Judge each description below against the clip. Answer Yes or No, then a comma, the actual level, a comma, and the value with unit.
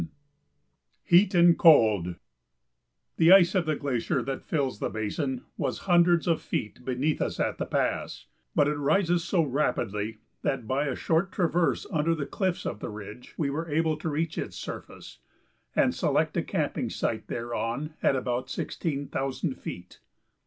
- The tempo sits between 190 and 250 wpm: No, average, 165 wpm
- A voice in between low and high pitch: Yes, medium, 145 Hz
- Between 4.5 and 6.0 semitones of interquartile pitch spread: Yes, average, 5.3 semitones